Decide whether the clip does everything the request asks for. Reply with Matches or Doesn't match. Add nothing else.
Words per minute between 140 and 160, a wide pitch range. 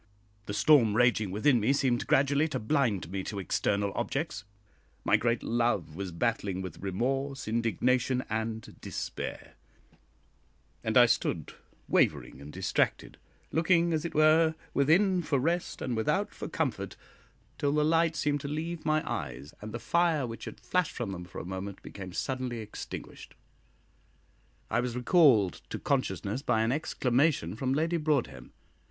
Matches